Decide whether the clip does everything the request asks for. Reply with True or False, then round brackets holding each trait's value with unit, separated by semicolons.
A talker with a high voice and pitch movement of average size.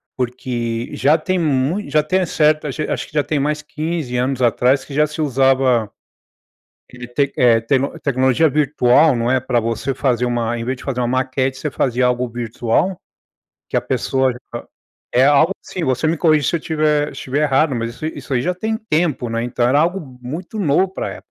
False (135 Hz; 3.7 semitones)